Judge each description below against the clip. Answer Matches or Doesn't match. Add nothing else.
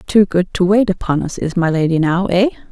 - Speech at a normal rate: Doesn't match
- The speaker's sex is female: Matches